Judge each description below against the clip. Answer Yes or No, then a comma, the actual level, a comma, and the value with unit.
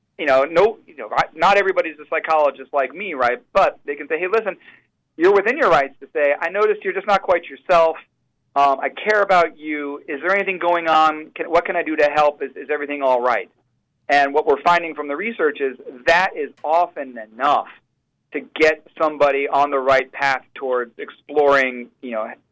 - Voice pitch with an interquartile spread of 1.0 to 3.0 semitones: No, average, 4.0 semitones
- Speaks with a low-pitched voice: No, medium, 155 Hz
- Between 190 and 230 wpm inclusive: Yes, fast, 205 wpm